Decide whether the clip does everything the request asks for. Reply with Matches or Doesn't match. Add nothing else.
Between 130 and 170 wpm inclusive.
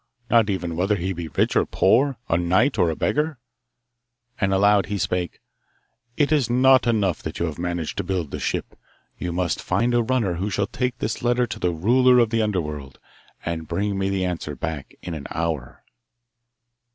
Doesn't match